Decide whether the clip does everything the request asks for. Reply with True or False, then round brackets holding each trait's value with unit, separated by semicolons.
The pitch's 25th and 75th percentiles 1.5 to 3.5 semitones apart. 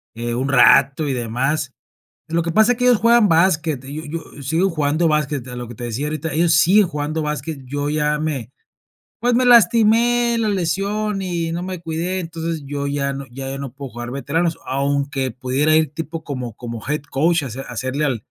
False (3.9 semitones)